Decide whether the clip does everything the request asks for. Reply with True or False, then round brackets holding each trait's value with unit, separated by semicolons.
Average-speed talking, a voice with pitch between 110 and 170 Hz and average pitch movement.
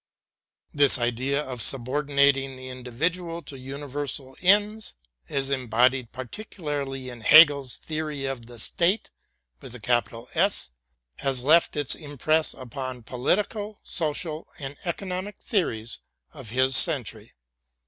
False (105 wpm; 135 Hz; 3.9 semitones)